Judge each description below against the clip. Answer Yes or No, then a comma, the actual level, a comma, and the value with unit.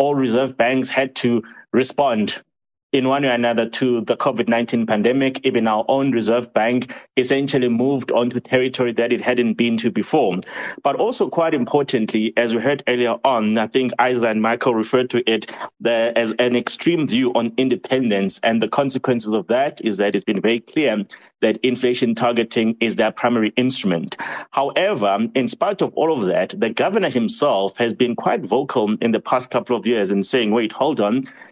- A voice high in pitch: No, low, 120 Hz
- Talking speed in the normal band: Yes, average, 185 wpm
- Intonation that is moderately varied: No, narrow, 2.1 semitones